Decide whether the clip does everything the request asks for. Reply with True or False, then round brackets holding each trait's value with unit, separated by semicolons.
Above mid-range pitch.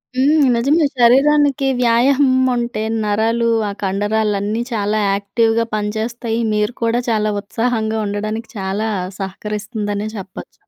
True (220 Hz)